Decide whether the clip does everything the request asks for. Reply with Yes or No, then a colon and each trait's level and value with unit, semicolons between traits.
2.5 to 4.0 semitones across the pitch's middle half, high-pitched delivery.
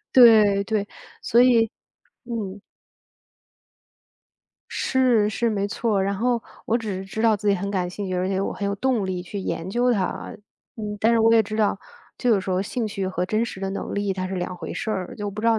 Yes: average, 2.8 semitones; high, 205 Hz